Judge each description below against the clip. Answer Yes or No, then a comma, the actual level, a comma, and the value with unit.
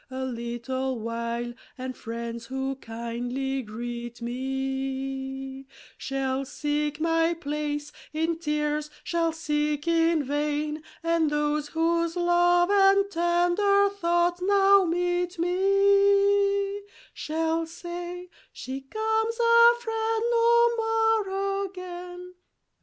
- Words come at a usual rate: No, slow, 100 wpm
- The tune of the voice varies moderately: No, wide, 6.4 semitones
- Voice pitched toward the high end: Yes, very high, 330 Hz